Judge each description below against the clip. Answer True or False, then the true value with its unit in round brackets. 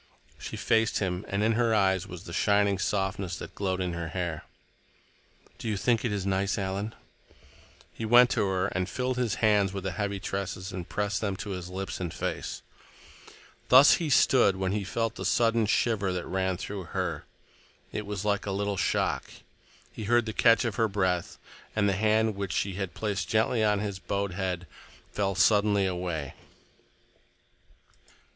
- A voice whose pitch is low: True (100 Hz)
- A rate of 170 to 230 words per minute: True (180 wpm)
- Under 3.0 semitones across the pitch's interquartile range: True (2.5 semitones)